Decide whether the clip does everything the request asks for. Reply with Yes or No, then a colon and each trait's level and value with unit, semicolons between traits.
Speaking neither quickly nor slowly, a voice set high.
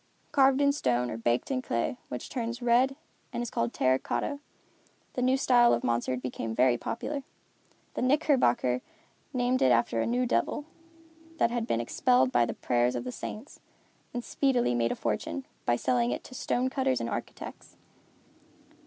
No: average, 170 wpm; low, 130 Hz